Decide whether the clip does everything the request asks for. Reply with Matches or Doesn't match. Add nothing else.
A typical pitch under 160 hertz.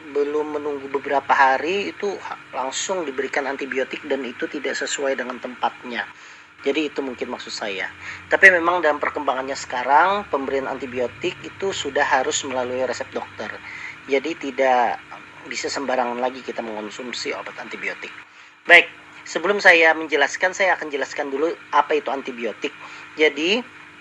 Matches